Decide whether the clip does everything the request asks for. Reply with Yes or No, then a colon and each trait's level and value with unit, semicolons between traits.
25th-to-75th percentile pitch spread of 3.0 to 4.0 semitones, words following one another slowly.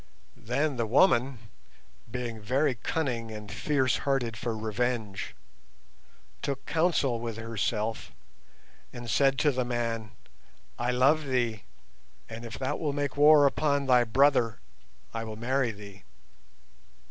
Yes: average, 3.4 semitones; slow, 125 wpm